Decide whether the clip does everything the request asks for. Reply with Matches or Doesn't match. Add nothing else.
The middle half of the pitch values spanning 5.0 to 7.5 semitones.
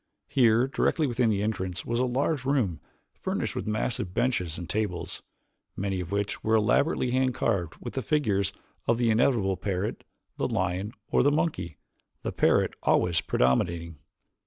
Matches